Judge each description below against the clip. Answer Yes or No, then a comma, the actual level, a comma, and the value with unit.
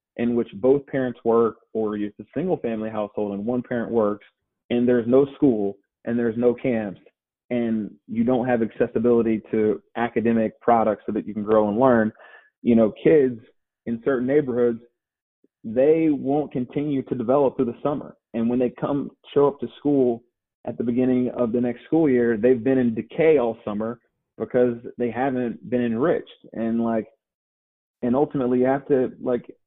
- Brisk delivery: No, average, 175 wpm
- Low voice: Yes, low, 120 Hz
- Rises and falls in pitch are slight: Yes, narrow, 2.3 semitones